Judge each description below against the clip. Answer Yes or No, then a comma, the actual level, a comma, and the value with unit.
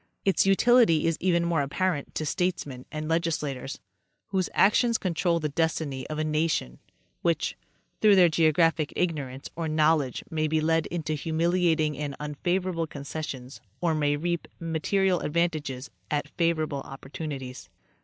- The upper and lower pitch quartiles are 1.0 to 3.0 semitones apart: Yes, average, 2.7 semitones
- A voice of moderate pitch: Yes, medium, 160 Hz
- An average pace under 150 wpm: Yes, average, 140 wpm